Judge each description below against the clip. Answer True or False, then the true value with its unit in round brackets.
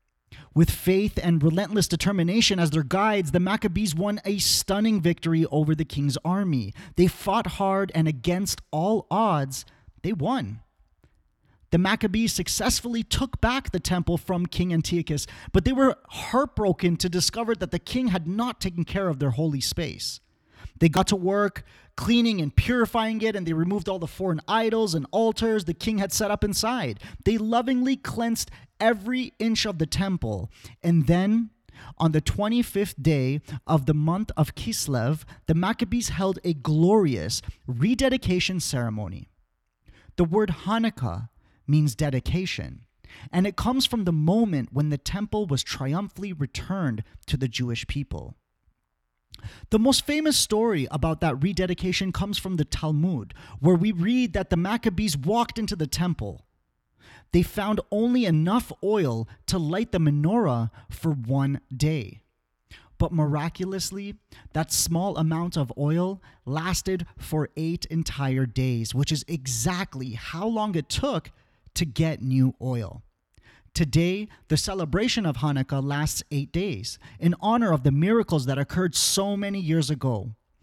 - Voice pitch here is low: False (170 Hz)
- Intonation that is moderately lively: False (6.3 semitones)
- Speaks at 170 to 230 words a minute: False (150 wpm)